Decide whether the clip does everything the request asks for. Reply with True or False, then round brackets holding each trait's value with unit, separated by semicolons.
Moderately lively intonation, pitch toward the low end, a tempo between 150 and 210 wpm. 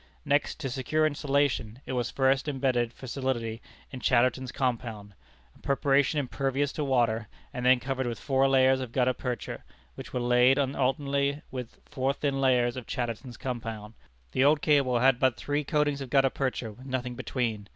False (2.1 semitones; 130 Hz; 175 wpm)